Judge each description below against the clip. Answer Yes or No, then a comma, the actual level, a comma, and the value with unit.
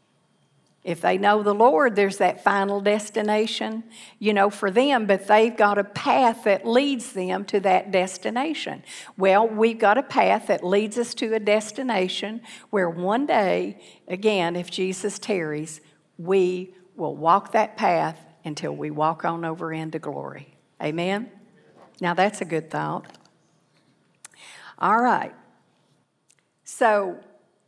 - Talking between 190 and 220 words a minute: No, slow, 135 wpm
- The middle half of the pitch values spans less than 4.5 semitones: Yes, average, 3.5 semitones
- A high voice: Yes, high, 200 Hz